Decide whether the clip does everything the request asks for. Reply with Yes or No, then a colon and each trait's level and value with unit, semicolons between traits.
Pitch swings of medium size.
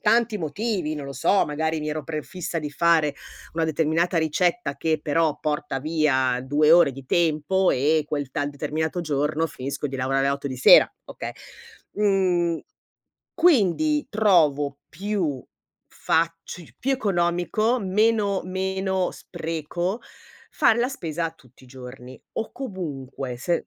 Yes: average, 4.5 semitones